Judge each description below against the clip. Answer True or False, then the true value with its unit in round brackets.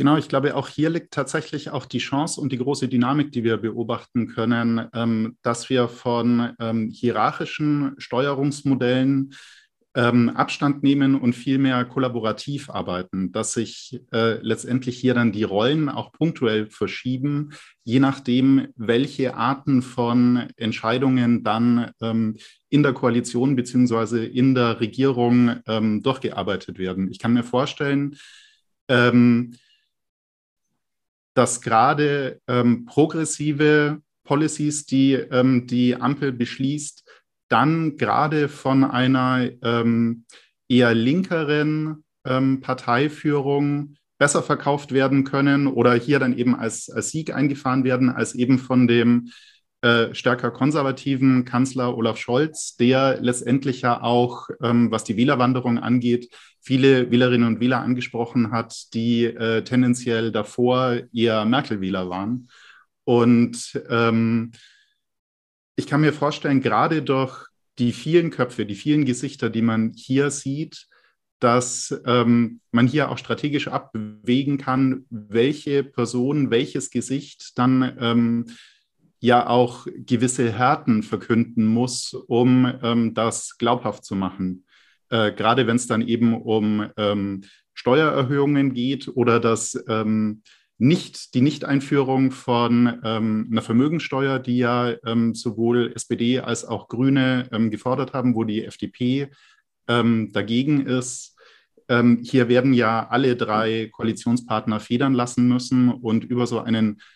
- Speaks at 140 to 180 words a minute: False (125 wpm)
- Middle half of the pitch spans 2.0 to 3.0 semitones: True (2.7 semitones)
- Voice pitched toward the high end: False (125 Hz)